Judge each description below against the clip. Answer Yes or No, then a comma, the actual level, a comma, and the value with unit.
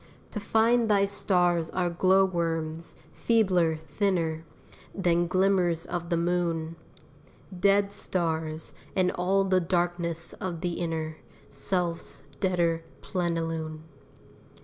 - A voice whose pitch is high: No, medium, 175 Hz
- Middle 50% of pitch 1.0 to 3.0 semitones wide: Yes, narrow, 2.4 semitones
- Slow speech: Yes, slow, 105 wpm